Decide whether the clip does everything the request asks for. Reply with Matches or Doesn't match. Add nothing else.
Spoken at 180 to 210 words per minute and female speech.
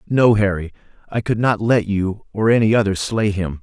Doesn't match